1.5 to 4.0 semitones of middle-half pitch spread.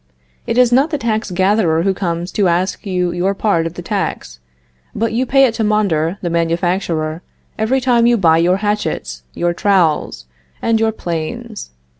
No: average, 4.8 semitones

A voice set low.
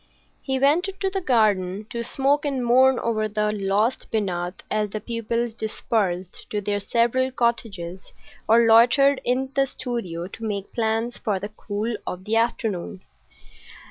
No: high, 225 Hz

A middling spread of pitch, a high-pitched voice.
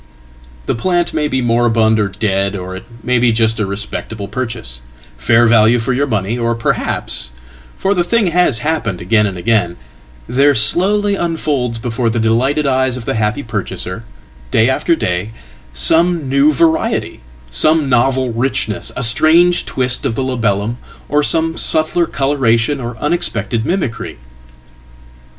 No: average, 5.0 semitones; low, 120 Hz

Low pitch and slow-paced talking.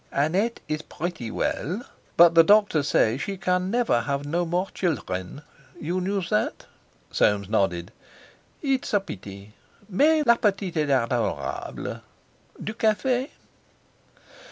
No: medium, 170 Hz; slow, 125 wpm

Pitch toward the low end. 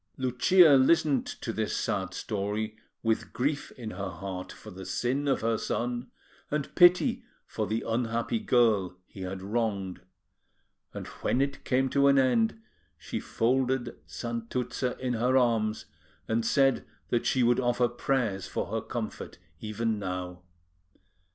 Yes: low, 120 Hz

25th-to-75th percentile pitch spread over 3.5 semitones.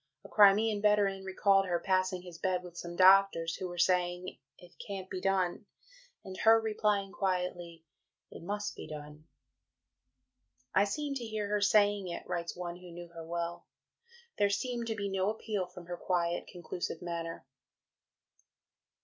No: average, 2.7 semitones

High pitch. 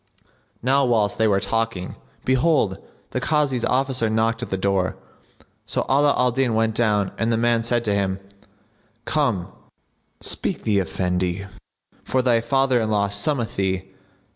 No: low, 115 Hz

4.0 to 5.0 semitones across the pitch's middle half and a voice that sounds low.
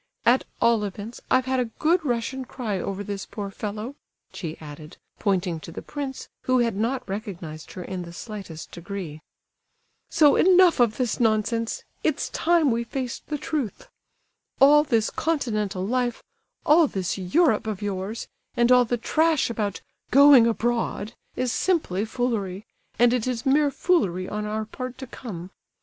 No: average, 4.7 semitones; high, 230 Hz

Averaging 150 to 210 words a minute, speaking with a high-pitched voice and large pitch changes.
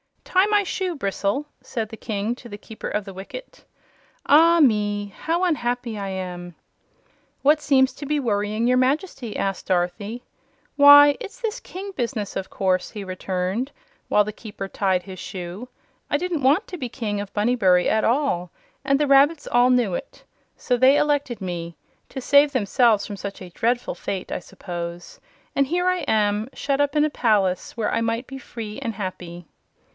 Yes: average, 180 wpm; high, 230 Hz; wide, 6.3 semitones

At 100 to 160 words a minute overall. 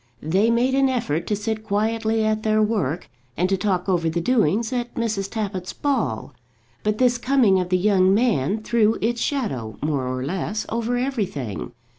No: average, 175 wpm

